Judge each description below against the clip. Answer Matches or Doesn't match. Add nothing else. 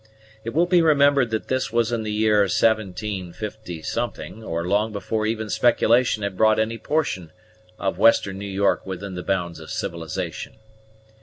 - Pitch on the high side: Doesn't match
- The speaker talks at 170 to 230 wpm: Doesn't match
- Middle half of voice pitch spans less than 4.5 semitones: Matches